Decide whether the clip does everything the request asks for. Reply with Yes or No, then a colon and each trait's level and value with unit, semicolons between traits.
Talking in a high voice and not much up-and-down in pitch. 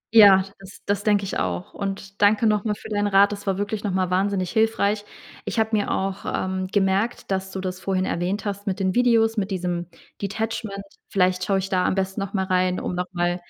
Yes: high, 195 Hz; narrow, 1.7 semitones